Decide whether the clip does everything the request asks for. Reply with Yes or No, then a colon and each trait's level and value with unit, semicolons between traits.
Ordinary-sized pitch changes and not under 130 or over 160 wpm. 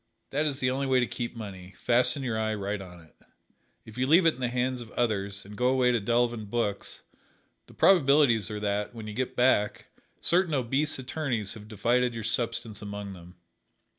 No: average, 3.8 semitones; average, 200 wpm